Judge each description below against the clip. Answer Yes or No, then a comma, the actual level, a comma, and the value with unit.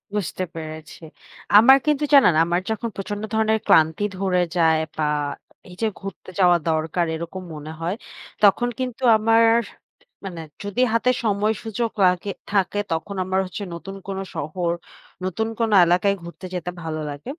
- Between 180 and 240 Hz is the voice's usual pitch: Yes, high, 190 Hz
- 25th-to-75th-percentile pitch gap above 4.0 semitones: Yes, average, 4.4 semitones